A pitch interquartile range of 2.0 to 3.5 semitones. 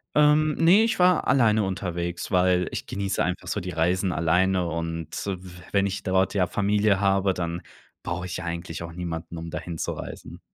Yes: average, 2.7 semitones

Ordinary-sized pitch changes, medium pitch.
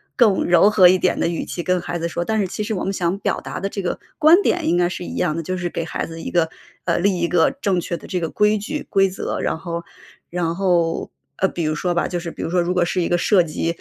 No: narrow, 2.3 semitones; medium, 175 Hz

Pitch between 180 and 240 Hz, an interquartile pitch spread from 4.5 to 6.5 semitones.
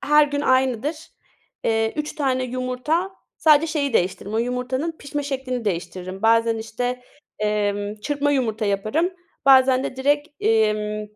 No: very high, 255 Hz; average, 4.8 semitones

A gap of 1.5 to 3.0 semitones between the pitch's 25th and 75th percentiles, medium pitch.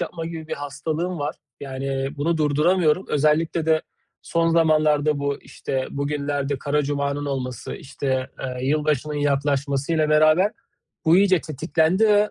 Yes: narrow, 2.4 semitones; medium, 150 Hz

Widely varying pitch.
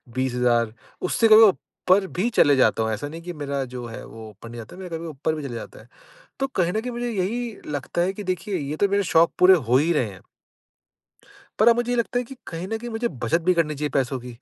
Yes: wide, 8.3 semitones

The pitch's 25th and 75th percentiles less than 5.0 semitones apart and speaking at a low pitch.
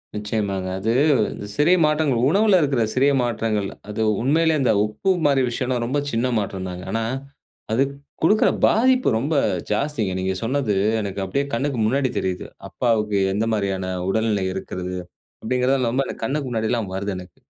No: average, 5.3 semitones; low, 115 Hz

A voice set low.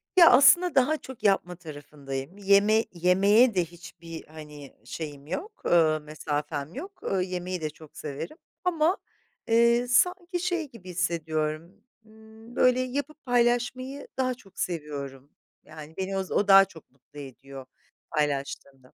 No: medium, 185 Hz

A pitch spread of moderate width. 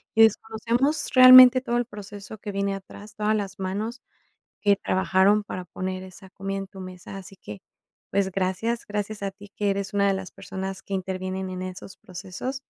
No: narrow, 2.2 semitones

